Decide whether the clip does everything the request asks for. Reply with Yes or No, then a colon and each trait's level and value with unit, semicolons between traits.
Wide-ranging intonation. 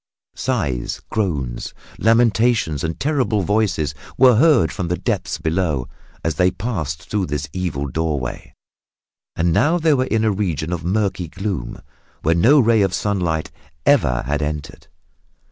Yes: wide, 6.2 semitones